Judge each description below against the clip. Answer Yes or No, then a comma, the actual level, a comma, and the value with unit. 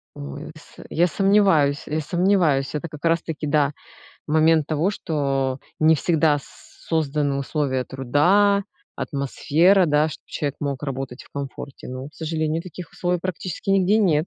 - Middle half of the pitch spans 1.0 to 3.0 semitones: No, average, 3.5 semitones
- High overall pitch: No, medium, 155 Hz